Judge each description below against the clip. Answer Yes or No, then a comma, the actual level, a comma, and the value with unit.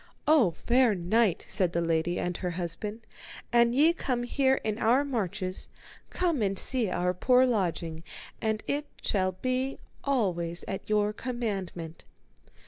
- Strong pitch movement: Yes, wide, 5.8 semitones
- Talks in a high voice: Yes, high, 210 Hz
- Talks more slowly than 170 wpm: Yes, average, 140 wpm